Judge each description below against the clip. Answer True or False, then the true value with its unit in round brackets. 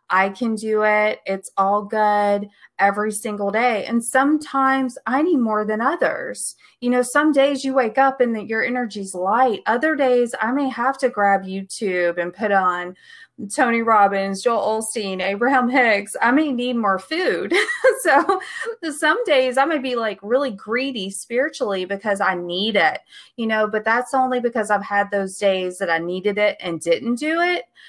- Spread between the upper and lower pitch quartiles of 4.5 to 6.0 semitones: True (4.8 semitones)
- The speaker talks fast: False (175 wpm)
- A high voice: True (230 Hz)